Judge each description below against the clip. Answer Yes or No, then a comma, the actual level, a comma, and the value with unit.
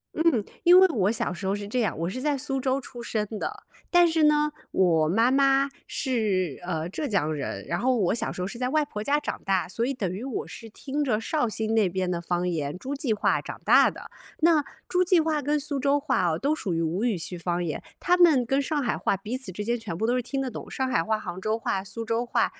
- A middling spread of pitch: No, wide, 6.9 semitones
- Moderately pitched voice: No, high, 230 Hz